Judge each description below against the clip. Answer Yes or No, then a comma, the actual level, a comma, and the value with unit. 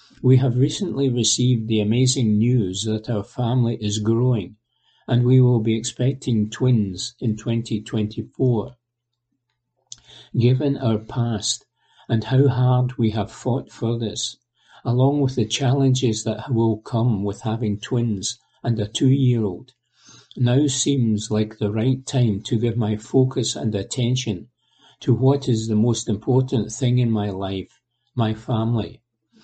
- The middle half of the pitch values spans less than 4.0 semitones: Yes, narrow, 2.6 semitones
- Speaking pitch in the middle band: No, low, 120 Hz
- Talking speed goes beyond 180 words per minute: No, average, 140 wpm